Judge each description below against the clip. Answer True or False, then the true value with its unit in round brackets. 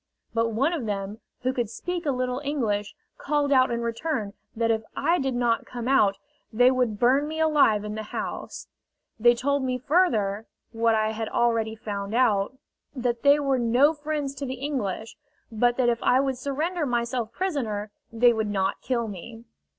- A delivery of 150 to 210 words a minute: True (180 wpm)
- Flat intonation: False (3.8 semitones)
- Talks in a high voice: True (240 Hz)